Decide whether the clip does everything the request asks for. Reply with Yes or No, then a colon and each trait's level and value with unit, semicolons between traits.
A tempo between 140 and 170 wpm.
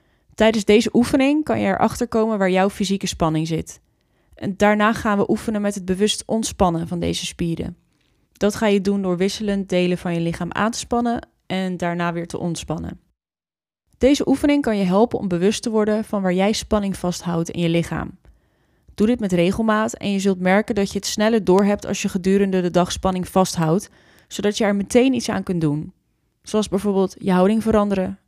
No: average, 195 wpm